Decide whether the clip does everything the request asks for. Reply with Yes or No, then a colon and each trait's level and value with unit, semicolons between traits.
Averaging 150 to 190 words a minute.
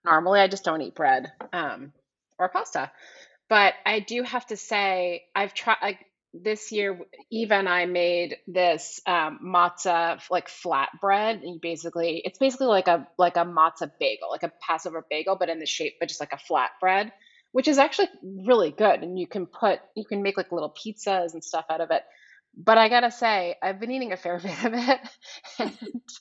No: average, 200 wpm